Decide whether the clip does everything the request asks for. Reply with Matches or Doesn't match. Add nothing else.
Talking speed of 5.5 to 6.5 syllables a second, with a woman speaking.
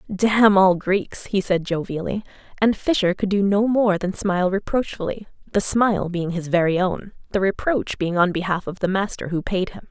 Doesn't match